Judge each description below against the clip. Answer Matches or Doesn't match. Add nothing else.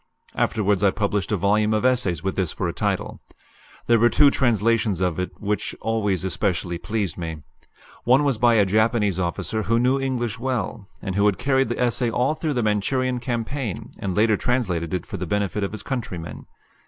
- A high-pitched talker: Doesn't match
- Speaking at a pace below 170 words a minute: Doesn't match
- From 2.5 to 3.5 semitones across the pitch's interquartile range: Doesn't match